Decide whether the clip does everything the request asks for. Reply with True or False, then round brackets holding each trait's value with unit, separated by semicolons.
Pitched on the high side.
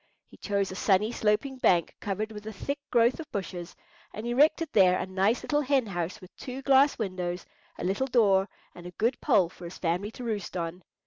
True (210 Hz)